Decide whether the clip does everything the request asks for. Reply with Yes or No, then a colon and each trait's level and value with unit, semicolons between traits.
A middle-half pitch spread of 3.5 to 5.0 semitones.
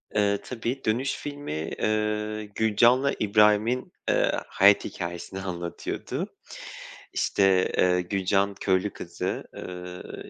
No: average, 2.8 semitones